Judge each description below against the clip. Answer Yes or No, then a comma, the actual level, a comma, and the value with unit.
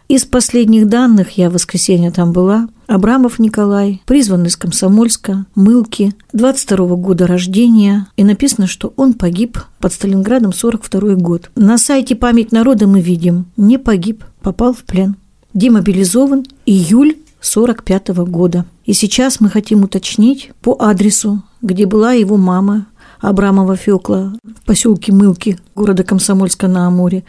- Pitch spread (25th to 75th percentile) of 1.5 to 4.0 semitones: Yes, average, 3.4 semitones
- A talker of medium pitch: No, high, 205 Hz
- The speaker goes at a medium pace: Yes, average, 135 wpm